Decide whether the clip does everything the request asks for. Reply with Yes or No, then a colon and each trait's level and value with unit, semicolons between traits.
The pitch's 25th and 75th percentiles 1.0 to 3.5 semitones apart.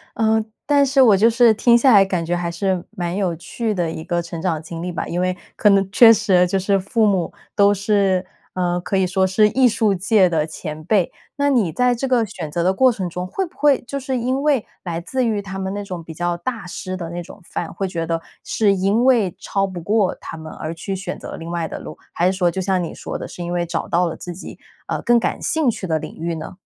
No: average, 4.2 semitones